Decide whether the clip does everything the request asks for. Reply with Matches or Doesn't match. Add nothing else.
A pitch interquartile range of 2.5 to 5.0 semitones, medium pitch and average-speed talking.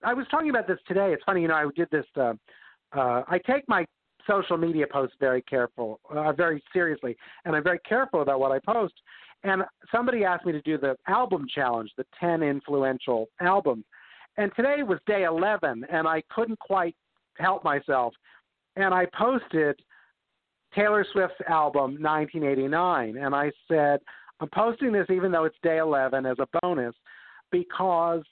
Doesn't match